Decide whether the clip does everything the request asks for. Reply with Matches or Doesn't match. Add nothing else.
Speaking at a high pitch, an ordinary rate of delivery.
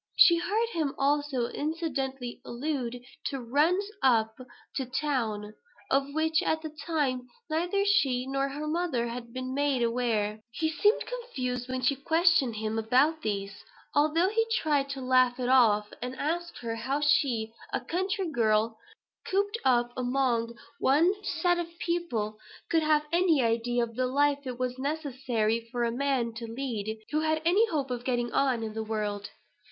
Matches